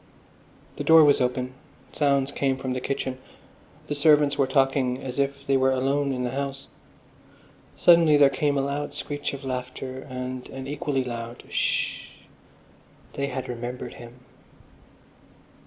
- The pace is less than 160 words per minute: Yes, average, 145 wpm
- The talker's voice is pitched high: No, low, 135 Hz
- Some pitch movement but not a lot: No, narrow, 1.8 semitones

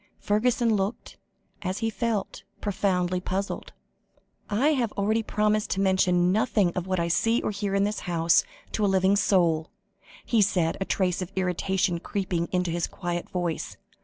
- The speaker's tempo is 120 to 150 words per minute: No, average, 160 wpm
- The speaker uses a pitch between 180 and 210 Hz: Yes, high, 190 Hz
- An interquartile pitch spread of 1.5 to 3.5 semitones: Yes, average, 2.8 semitones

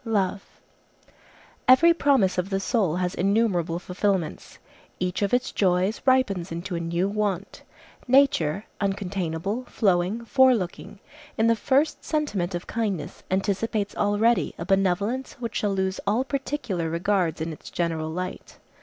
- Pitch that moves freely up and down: No, average, 4.3 semitones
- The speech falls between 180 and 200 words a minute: No, slow, 135 wpm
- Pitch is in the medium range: No, high, 195 Hz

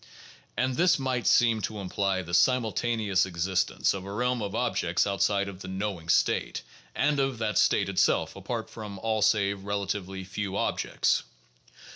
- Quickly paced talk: No, average, 160 wpm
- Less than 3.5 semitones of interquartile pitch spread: Yes, average, 3.0 semitones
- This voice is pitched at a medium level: No, low, 100 Hz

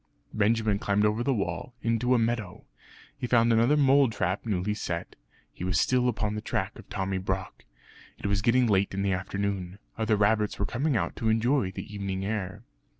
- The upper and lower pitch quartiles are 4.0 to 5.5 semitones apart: No, average, 3.2 semitones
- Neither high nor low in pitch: No, low, 105 Hz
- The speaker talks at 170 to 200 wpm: Yes, average, 190 wpm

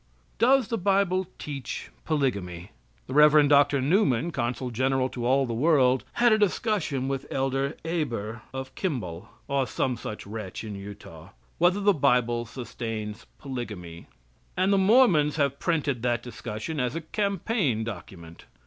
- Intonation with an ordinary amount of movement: No, wide, 6.1 semitones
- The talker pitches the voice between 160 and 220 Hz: No, low, 135 Hz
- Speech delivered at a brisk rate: No, average, 145 wpm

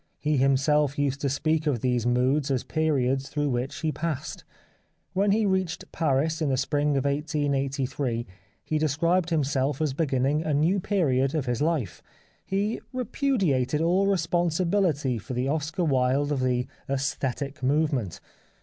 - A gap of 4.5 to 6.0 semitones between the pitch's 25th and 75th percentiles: No, average, 3.4 semitones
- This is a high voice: No, medium, 145 Hz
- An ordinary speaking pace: Yes, average, 150 wpm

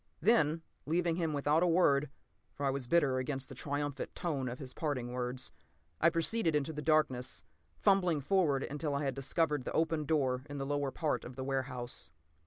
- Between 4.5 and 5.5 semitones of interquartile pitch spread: No, average, 3.4 semitones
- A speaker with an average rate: Yes, average, 190 wpm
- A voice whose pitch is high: No, medium, 145 Hz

